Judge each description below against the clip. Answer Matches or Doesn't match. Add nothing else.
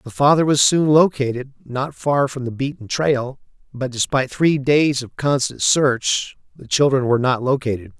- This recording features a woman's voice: Doesn't match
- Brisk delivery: Doesn't match